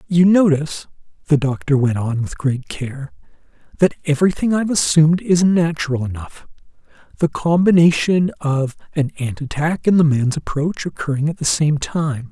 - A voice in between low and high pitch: Yes, medium, 155 Hz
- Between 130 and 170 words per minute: Yes, average, 150 wpm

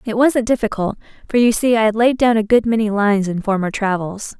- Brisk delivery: Yes, fast, 230 wpm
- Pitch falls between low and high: No, high, 220 Hz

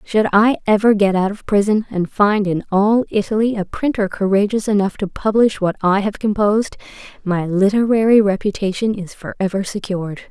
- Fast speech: No, average, 165 wpm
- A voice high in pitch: Yes, high, 205 Hz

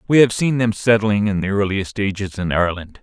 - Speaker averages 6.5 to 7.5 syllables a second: No, 5.6 syllables/s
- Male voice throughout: Yes, male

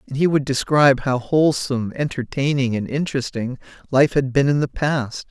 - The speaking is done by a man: Yes, male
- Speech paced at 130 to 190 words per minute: Yes, average, 170 wpm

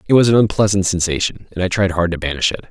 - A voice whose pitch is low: Yes, very low, 95 Hz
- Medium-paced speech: No, fast, 265 wpm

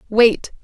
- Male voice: No, female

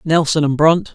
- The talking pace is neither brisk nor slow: Yes, average, 190 wpm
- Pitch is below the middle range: No, medium, 155 Hz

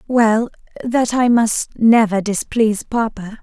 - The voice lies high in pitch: Yes, high, 225 Hz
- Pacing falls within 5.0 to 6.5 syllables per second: No, 3.9 syllables/s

